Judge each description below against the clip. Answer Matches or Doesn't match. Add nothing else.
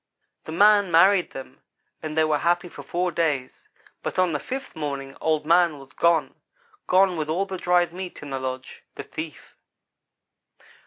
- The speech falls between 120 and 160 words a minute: Doesn't match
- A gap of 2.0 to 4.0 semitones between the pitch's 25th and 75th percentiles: Matches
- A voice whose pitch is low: Doesn't match